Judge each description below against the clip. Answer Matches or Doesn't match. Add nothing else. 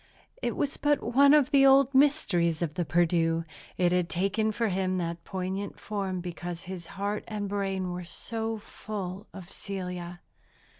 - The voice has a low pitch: Doesn't match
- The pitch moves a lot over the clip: Doesn't match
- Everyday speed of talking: Matches